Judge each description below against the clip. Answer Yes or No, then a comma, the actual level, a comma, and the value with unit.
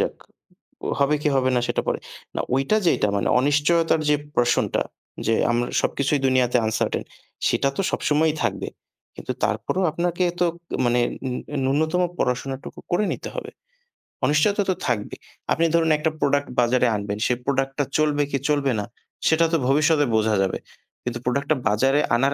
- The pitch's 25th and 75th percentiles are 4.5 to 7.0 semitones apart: No, average, 3.9 semitones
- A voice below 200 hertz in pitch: Yes, medium, 140 Hz